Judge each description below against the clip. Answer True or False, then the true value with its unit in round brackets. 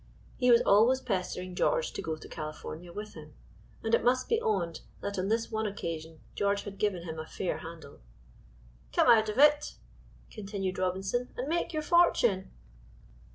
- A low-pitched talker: False (200 Hz)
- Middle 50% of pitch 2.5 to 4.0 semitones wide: False (5.2 semitones)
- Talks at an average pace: True (170 wpm)